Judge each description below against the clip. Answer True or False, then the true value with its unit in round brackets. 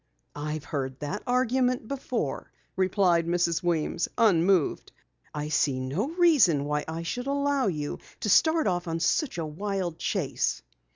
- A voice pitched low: False (175 Hz)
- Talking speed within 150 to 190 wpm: False (140 wpm)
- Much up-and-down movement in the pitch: True (8.2 semitones)